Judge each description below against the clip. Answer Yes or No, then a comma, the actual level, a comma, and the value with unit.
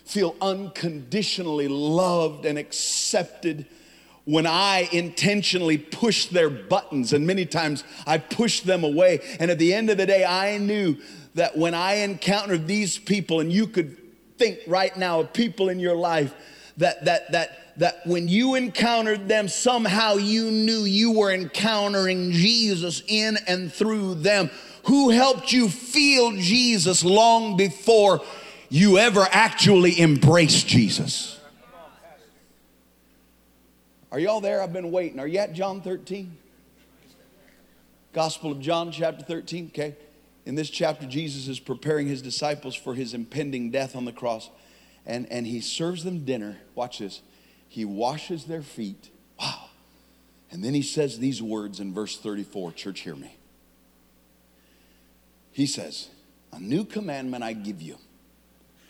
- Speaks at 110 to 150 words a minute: Yes, average, 145 wpm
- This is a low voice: No, medium, 170 Hz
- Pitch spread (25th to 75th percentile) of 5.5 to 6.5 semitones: Yes, wide, 5.8 semitones